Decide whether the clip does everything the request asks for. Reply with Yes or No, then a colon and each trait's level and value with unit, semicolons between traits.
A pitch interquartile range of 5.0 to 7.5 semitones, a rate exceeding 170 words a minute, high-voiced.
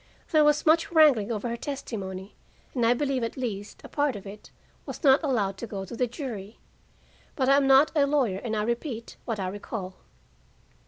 Yes: wide, 5.4 semitones; average, 200 wpm; high, 235 Hz